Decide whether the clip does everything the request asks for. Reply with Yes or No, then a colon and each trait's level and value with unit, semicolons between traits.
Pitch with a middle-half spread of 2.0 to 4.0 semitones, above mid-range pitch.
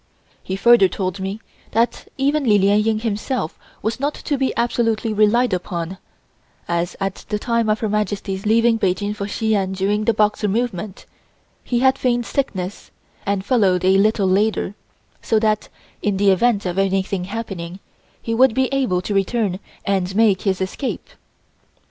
Yes: average, 3.2 semitones; high, 210 Hz